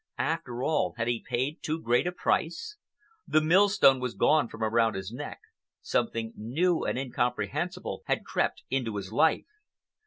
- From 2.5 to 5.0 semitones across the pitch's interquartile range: No, wide, 5.5 semitones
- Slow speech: No, average, 155 wpm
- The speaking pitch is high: No, low, 130 Hz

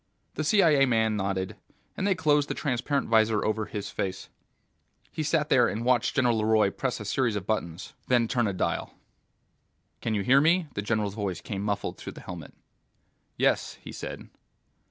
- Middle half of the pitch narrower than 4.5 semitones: No, average, 5.0 semitones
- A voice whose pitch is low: Yes, low, 110 Hz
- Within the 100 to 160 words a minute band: No, average, 175 wpm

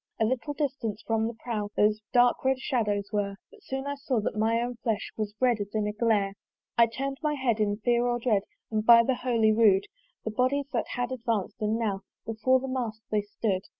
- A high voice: Yes, high, 230 Hz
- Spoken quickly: Yes, fast, 215 wpm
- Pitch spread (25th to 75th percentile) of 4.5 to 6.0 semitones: No, average, 3.1 semitones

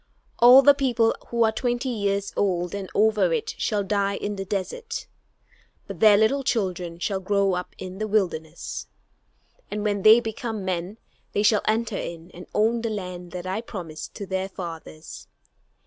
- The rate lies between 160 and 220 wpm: Yes, average, 170 wpm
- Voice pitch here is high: Yes, high, 200 Hz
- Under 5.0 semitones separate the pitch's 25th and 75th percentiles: Yes, average, 3.3 semitones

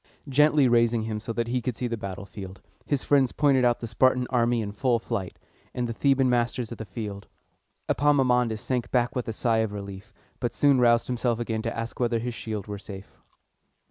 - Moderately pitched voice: No, low, 120 Hz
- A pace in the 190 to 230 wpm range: Yes, fast, 205 wpm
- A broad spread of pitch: No, narrow, 2.4 semitones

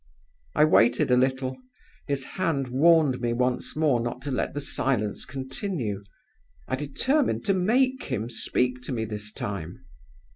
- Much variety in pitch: No, average, 4.3 semitones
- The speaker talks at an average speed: Yes, average, 150 wpm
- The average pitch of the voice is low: Yes, low, 130 Hz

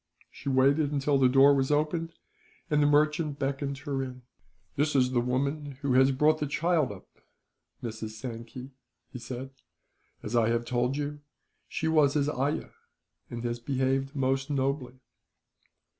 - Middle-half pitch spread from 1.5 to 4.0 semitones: Yes, narrow, 2.5 semitones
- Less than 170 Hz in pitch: Yes, low, 135 Hz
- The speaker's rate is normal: Yes, average, 155 wpm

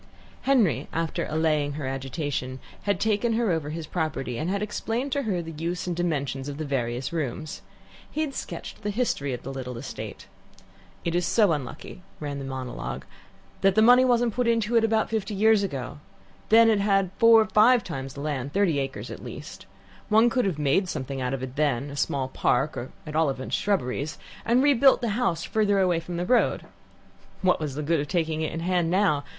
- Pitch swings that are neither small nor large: No, wide, 7.1 semitones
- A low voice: No, medium, 165 Hz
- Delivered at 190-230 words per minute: Yes, average, 200 wpm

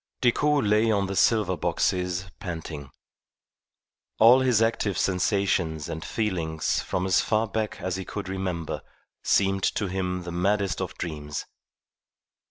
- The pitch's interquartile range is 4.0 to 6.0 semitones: No, average, 3.2 semitones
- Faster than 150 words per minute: No, slow, 135 wpm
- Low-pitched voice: Yes, very low, 95 Hz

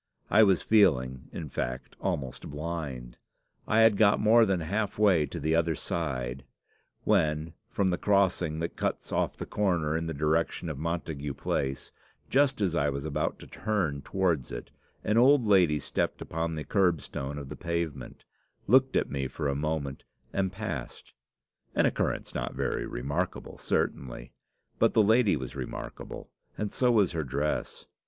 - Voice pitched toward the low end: Yes, very low, 80 Hz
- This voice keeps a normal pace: Yes, average, 160 wpm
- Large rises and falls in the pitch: Yes, wide, 5.7 semitones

